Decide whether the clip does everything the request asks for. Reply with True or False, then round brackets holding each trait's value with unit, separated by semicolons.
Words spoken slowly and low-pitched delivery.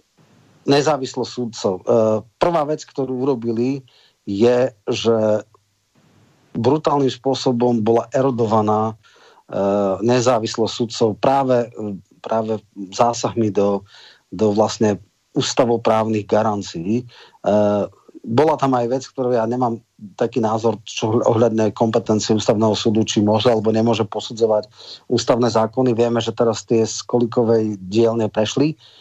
True (105 wpm; 115 Hz)